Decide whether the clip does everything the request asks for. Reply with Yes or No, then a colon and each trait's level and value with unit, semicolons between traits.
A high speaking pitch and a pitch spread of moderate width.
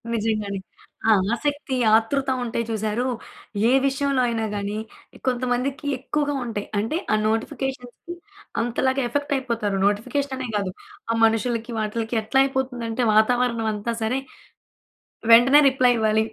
Yes: high, 240 Hz; average, 3.2 semitones